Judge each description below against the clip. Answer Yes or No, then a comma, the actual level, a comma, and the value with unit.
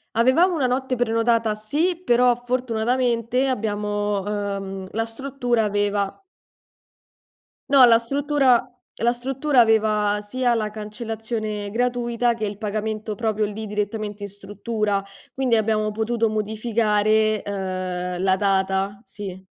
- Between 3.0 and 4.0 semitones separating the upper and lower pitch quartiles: No, narrow, 2.6 semitones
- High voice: Yes, high, 220 Hz